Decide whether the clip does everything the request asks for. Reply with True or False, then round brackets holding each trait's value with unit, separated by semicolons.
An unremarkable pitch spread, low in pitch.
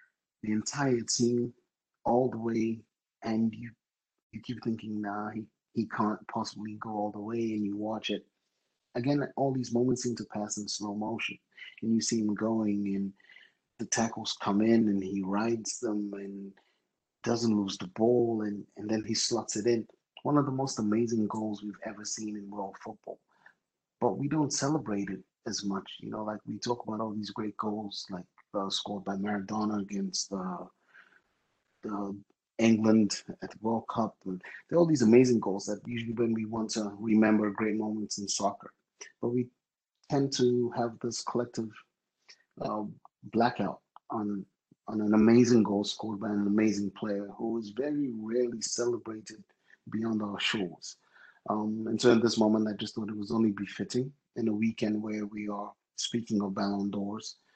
False (2.0 semitones; 110 Hz)